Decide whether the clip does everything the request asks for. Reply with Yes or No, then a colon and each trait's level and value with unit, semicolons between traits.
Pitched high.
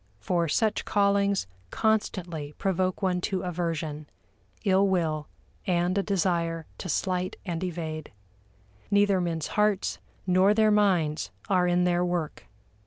No: medium, 180 Hz